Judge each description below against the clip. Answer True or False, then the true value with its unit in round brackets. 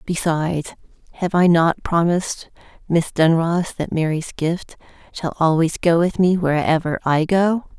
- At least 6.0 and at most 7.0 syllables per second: False (4.4 syllables/s)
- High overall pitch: False (170 Hz)